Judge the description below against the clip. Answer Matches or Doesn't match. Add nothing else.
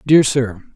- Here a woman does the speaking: Doesn't match